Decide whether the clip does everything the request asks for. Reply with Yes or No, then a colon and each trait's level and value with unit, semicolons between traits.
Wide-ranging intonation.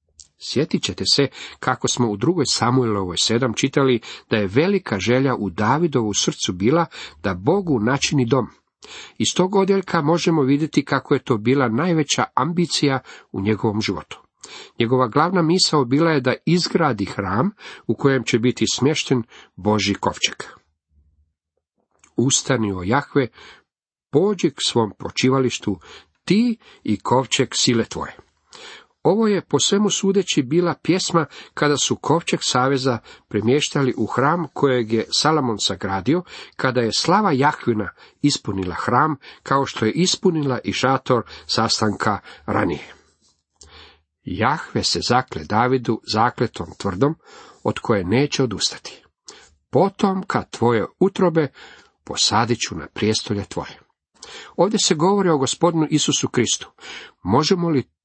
Yes: wide, 6.5 semitones